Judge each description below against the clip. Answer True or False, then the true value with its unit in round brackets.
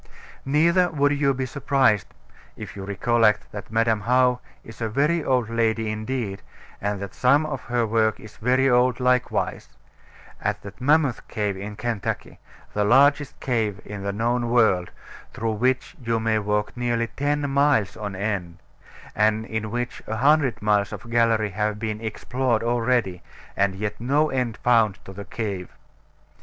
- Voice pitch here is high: False (115 Hz)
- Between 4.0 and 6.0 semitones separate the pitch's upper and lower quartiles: False (3.4 semitones)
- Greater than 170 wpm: False (160 wpm)